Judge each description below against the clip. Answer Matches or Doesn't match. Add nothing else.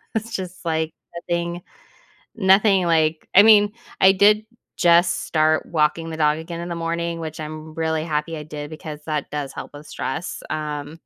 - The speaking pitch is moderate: Matches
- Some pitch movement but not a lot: Doesn't match